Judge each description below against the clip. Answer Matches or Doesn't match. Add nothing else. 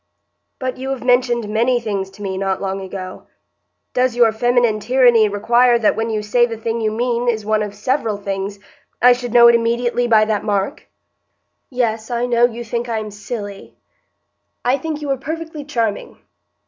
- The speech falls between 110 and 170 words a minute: Doesn't match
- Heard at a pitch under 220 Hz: Doesn't match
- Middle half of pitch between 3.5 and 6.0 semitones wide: Doesn't match